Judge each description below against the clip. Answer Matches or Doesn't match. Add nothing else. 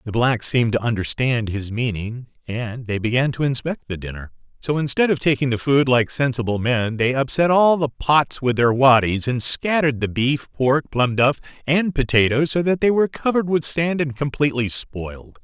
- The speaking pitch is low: Matches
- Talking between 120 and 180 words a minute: Doesn't match